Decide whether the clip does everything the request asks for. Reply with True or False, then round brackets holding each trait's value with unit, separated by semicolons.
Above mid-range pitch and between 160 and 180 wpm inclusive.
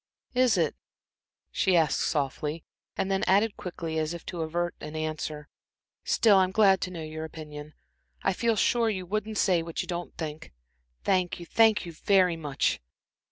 False (175 Hz; 170 wpm)